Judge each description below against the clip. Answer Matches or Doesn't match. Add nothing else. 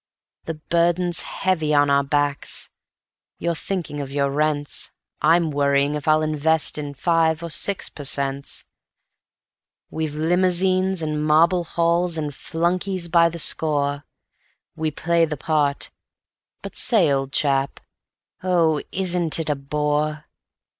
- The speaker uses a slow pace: Matches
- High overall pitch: Doesn't match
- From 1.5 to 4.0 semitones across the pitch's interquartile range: Matches